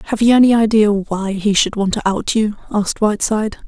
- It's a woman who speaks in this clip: Yes, female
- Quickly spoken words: Yes, fast, 210 wpm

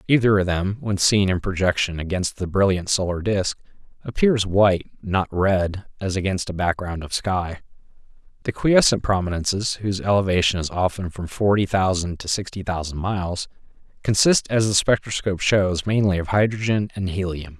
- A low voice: Yes, very low, 95 Hz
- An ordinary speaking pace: Yes, average, 155 wpm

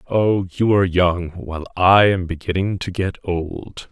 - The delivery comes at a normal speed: Yes, average, 170 wpm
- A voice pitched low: Yes, very low, 90 Hz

